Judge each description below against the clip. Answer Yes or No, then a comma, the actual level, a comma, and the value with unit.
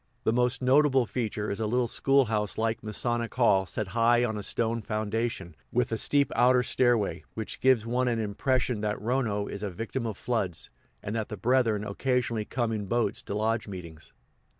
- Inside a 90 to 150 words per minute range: No, average, 190 wpm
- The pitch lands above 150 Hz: No, low, 115 Hz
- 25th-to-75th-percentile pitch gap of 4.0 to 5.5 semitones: No, average, 2.8 semitones